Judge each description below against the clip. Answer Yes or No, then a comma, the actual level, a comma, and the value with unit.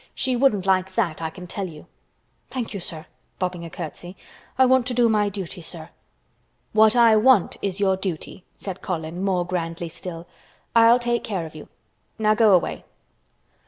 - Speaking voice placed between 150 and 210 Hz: Yes, high, 190 Hz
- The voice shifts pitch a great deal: No, average, 4.2 semitones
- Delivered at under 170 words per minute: No, average, 175 wpm